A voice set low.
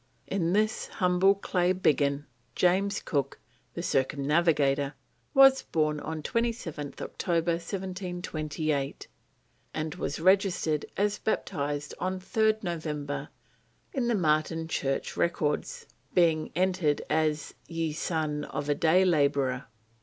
No: medium, 160 Hz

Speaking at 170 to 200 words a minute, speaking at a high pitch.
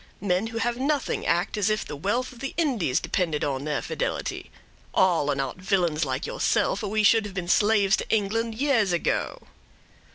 Yes: average, 190 wpm; high, 200 Hz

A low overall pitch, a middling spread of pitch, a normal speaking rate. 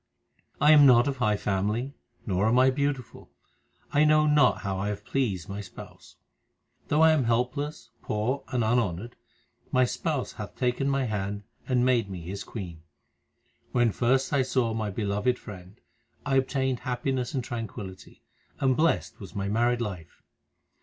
Yes: low, 120 Hz; average, 4.4 semitones; average, 160 wpm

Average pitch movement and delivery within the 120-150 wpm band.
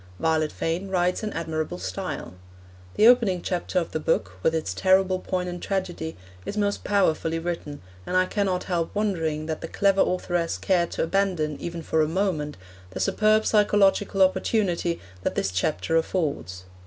No: average, 3.4 semitones; average, 160 wpm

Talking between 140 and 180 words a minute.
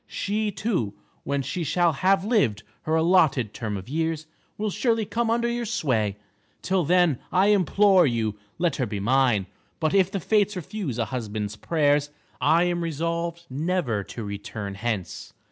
Yes: average, 160 wpm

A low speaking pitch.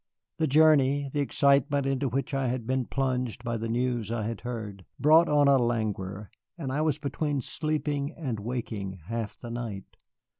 Yes: low, 130 Hz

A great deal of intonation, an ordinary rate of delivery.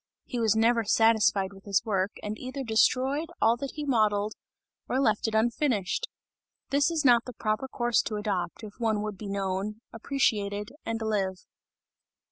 No: average, 3.0 semitones; average, 165 wpm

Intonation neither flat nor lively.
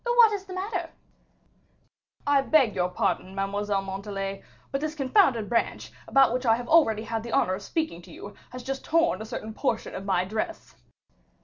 No: wide, 7.7 semitones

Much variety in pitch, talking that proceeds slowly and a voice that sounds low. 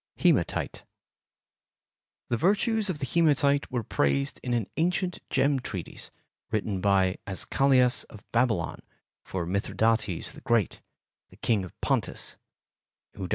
Yes: wide, 6.4 semitones; slow, 115 wpm; low, 120 Hz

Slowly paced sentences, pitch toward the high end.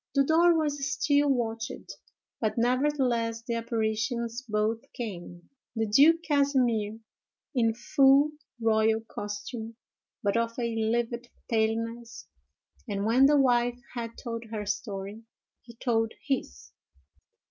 Yes: slow, 115 wpm; high, 230 Hz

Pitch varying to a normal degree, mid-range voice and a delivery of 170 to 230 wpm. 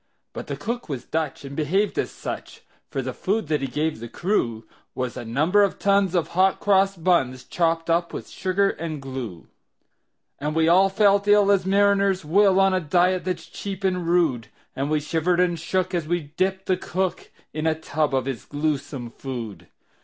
Yes: average, 4.6 semitones; medium, 170 Hz; average, 190 wpm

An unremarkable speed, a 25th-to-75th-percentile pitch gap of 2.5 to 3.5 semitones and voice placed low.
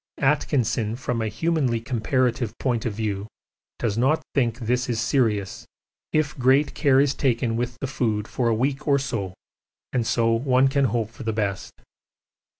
Yes: average, 165 wpm; average, 3.0 semitones; low, 120 Hz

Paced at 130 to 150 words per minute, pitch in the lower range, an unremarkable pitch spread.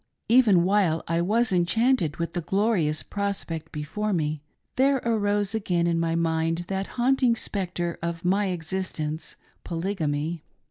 No: average, 145 wpm; medium, 180 Hz; average, 3.9 semitones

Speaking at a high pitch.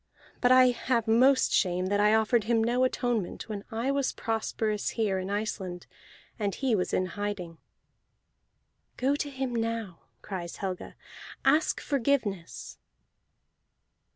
Yes: high, 220 Hz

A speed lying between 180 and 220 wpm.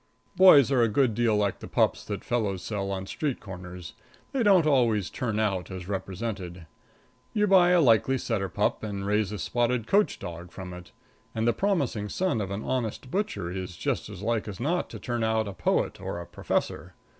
Yes: average, 200 wpm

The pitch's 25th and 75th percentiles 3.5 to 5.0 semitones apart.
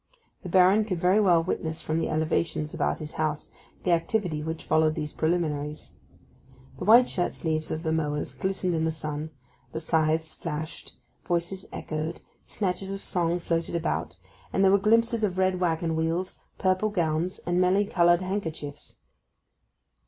No: average, 2.8 semitones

